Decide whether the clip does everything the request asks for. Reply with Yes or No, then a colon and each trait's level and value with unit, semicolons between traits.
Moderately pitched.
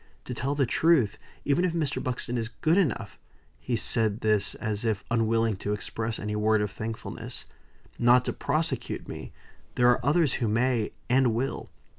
No: low, 120 Hz